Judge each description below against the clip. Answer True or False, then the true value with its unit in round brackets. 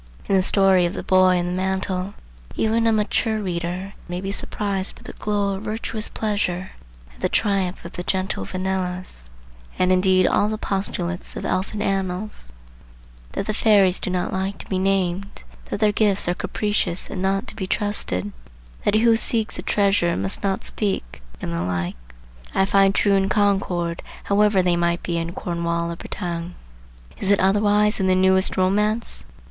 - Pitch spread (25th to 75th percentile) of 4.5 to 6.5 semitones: False (2.6 semitones)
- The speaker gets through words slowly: False (175 wpm)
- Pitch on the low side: False (190 Hz)